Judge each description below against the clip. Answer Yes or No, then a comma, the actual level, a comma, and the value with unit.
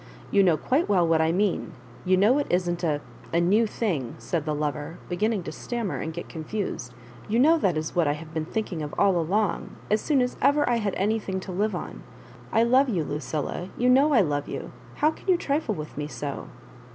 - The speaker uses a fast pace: Yes, fast, 230 wpm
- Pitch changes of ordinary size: No, wide, 6.1 semitones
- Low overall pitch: No, medium, 185 Hz